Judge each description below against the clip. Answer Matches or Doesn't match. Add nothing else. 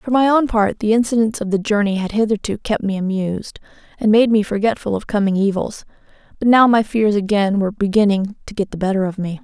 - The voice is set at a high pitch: Matches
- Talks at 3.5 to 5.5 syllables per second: Doesn't match